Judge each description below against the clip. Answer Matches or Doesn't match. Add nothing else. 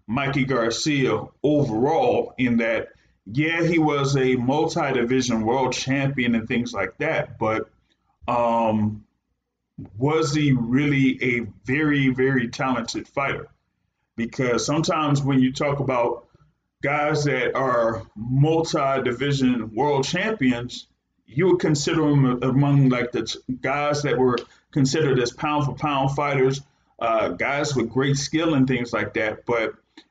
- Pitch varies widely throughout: Doesn't match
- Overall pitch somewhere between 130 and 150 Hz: Matches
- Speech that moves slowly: Matches